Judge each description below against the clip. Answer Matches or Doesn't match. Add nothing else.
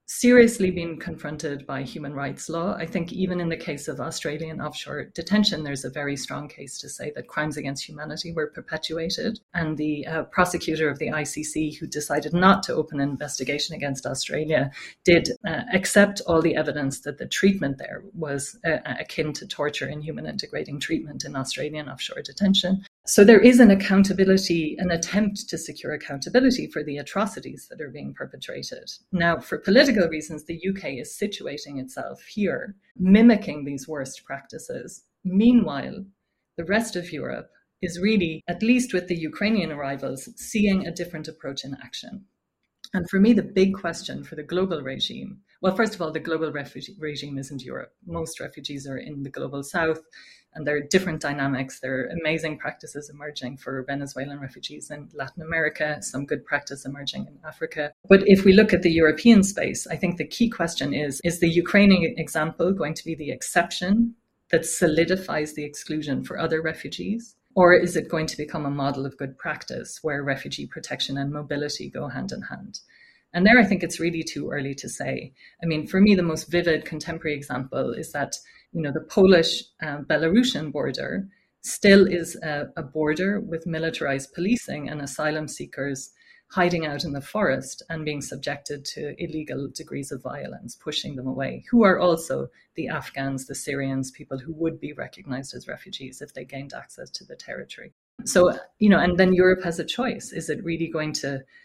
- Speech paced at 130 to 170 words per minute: Doesn't match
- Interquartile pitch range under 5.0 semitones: Matches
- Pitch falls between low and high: Matches